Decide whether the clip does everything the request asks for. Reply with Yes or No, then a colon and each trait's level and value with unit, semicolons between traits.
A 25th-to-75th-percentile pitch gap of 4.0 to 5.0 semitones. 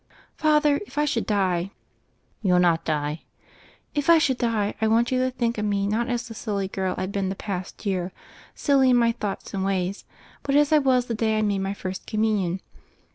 Yes: average, 4.5 semitones